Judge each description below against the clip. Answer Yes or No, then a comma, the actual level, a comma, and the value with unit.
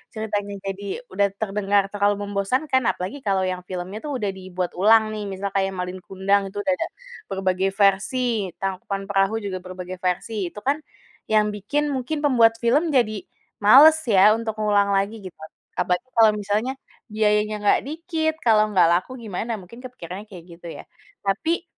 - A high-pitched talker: Yes, high, 205 Hz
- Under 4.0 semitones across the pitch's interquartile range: Yes, average, 2.8 semitones